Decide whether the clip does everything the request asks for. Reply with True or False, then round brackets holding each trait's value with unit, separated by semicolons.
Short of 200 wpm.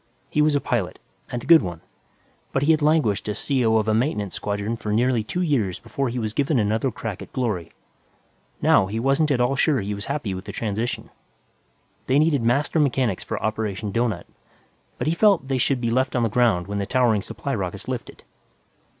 False (205 wpm)